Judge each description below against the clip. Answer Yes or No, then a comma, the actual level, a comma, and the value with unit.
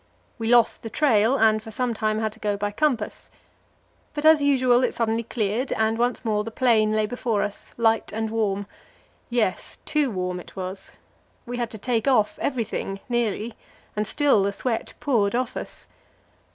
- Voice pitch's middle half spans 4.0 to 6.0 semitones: No, average, 2.7 semitones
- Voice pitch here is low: No, high, 225 Hz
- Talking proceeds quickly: No, average, 180 wpm